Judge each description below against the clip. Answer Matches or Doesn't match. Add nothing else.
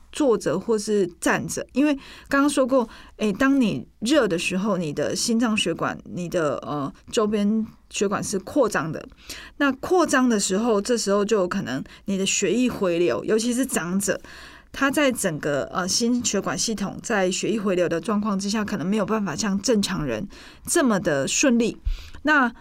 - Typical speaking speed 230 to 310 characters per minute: Matches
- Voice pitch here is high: Matches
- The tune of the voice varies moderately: Matches